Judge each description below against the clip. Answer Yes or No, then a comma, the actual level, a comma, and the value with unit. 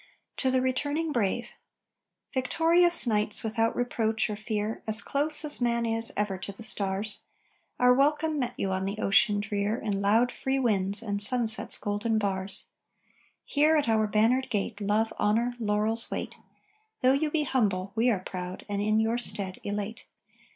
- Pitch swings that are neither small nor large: Yes, average, 3.5 semitones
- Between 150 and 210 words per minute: Yes, average, 165 wpm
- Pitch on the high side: Yes, high, 220 Hz